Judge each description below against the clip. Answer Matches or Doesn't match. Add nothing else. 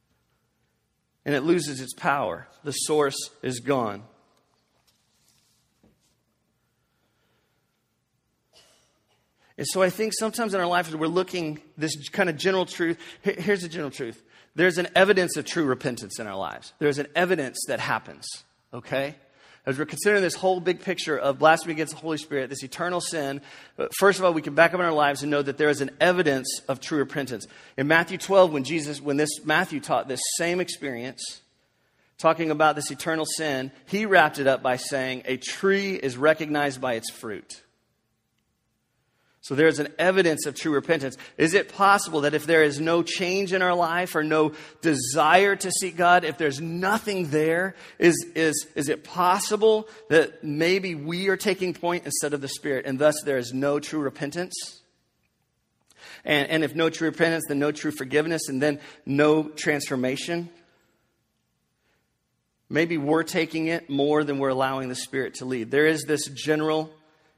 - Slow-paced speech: Doesn't match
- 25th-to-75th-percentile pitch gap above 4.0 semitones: Doesn't match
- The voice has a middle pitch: Matches